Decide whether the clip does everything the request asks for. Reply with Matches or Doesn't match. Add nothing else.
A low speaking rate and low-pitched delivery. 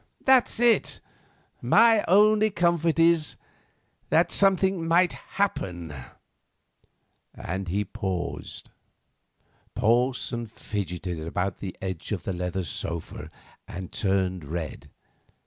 Matches